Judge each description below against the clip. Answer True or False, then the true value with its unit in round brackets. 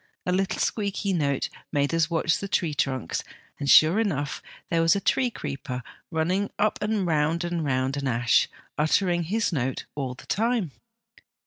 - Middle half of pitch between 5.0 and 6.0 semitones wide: True (5.6 semitones)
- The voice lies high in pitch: False (165 Hz)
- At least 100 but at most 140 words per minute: False (165 wpm)